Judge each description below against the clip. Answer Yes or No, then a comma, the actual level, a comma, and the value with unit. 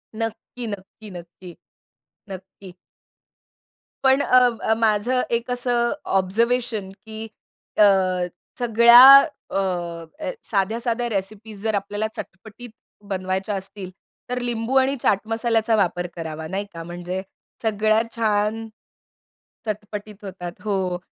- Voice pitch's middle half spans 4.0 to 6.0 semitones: No, average, 3.3 semitones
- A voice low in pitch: No, high, 210 Hz